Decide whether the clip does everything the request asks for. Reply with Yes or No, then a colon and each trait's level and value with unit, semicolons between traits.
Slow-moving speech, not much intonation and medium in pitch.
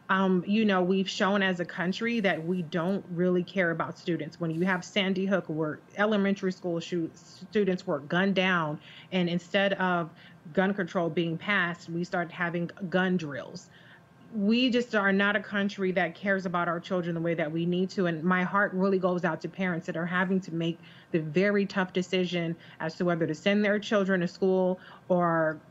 No: average, 195 wpm; narrow, 2.1 semitones; medium, 180 Hz